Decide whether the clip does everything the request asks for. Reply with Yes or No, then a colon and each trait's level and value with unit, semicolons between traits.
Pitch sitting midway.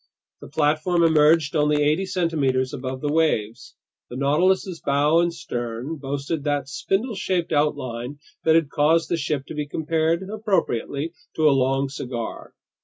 Yes: medium, 150 Hz